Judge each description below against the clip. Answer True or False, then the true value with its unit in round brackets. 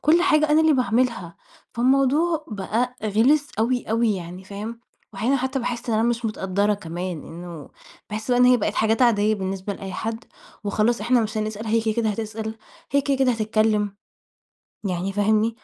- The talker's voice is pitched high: True (220 Hz)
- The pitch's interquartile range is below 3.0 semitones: False (3.4 semitones)